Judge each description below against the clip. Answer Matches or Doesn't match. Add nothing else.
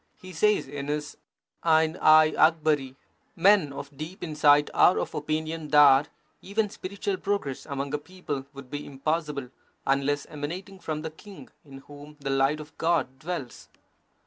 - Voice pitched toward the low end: Doesn't match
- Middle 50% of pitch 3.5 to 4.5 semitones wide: Doesn't match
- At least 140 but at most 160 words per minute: Matches